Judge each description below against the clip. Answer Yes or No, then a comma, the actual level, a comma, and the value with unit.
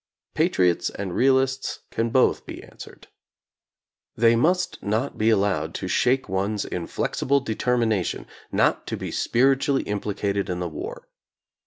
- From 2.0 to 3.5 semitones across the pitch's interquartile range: No, average, 5.1 semitones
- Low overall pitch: Yes, low, 110 Hz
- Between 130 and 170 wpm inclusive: Yes, average, 140 wpm